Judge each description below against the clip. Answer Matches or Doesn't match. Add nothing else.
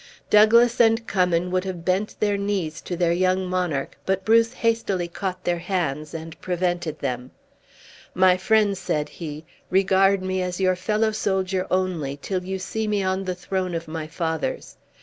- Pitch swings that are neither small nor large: Doesn't match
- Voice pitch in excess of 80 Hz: Matches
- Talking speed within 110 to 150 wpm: Doesn't match